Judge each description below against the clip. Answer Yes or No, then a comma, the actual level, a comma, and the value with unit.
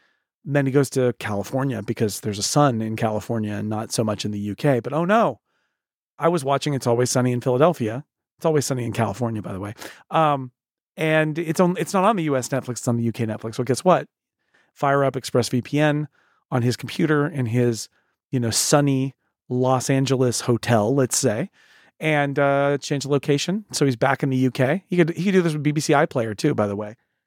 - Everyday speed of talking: No, fast, 210 wpm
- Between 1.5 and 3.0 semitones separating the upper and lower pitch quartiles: No, average, 4.0 semitones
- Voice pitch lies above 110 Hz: Yes, low, 135 Hz